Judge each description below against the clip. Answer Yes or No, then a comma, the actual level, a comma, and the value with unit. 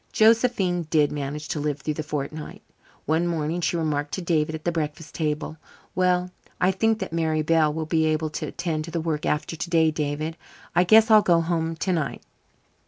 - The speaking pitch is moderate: Yes, medium, 160 Hz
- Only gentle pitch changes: Yes, narrow, 2.3 semitones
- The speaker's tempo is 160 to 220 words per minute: Yes, average, 190 wpm